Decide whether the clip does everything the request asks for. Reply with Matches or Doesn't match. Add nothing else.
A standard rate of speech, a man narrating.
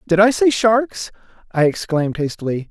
Matches